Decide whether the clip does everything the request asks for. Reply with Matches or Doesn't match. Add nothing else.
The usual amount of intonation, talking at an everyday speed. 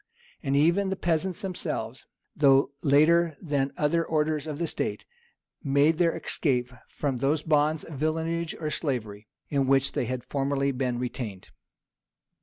Matches